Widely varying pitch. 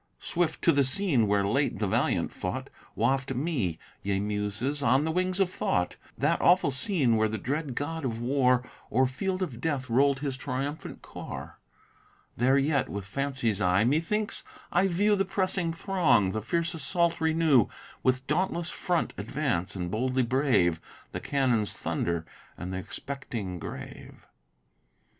Yes: wide, 6.8 semitones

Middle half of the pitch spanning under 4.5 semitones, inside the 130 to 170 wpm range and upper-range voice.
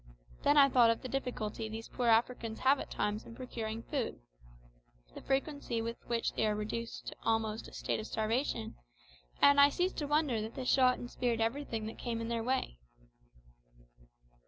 No: average, 2.9 semitones; average, 180 wpm; high, 230 Hz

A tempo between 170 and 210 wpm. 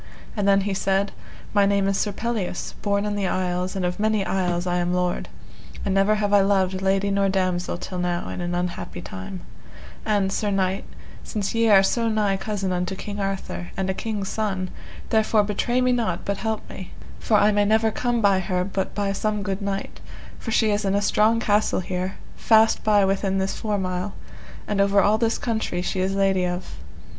Yes: fast, 205 wpm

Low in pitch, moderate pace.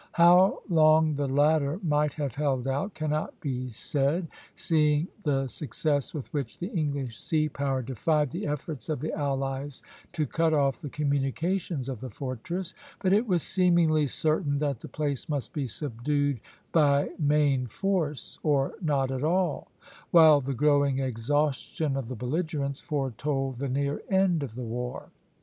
No: medium, 145 Hz; average, 155 wpm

